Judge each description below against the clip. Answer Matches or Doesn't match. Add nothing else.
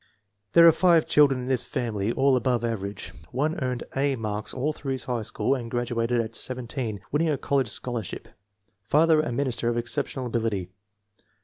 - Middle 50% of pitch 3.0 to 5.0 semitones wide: Matches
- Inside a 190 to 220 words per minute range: Doesn't match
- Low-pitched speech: Matches